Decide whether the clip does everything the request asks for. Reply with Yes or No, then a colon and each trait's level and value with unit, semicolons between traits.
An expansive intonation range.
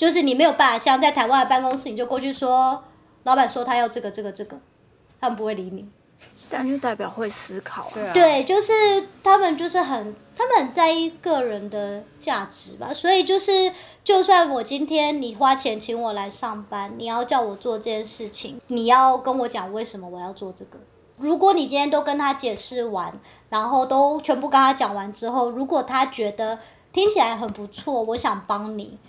No: average, 5.0 semitones